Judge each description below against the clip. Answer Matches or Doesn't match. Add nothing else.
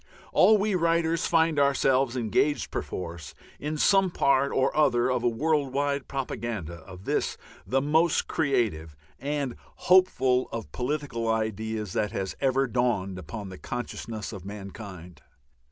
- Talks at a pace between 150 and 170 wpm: Doesn't match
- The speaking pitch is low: Matches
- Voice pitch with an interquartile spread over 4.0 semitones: Matches